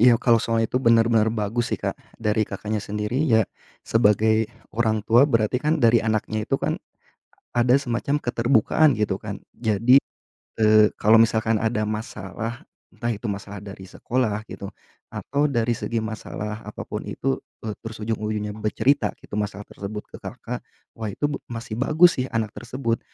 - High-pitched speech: No, low, 110 Hz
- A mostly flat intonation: Yes, narrow, 2.0 semitones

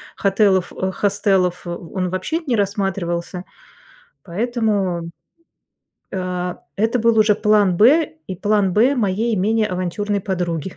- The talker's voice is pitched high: Yes, high, 200 Hz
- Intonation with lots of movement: No, average, 3.0 semitones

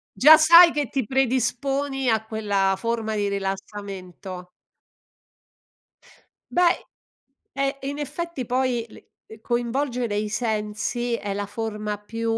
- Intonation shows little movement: No, average, 4.5 semitones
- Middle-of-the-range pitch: No, high, 230 Hz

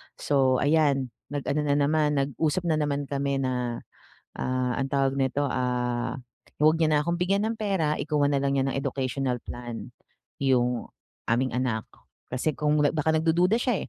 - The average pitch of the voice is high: No, medium, 140 Hz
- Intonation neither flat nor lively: Yes, average, 3.1 semitones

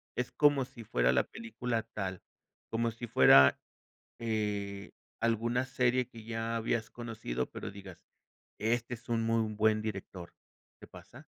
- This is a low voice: Yes, low, 115 Hz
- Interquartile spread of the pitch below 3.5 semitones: Yes, narrow, 2.5 semitones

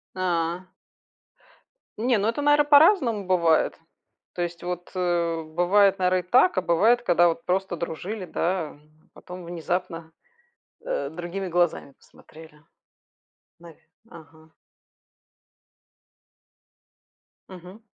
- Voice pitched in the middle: Yes, medium, 180 Hz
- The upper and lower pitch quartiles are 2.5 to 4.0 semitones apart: Yes, average, 2.9 semitones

